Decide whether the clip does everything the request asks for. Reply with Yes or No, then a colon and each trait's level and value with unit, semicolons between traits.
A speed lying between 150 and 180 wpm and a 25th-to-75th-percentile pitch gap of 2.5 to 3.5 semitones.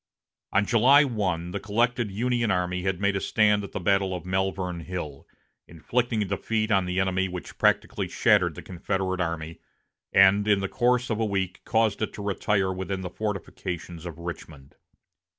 Yes: average, 170 wpm; average, 2.9 semitones